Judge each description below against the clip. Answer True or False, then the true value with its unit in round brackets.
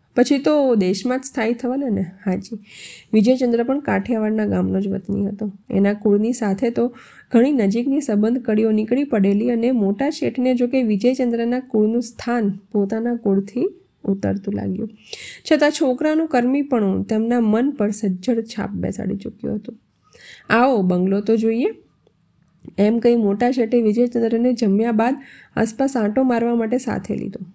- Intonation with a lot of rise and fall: False (3.2 semitones)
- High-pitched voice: True (230 Hz)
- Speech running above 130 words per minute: True (140 wpm)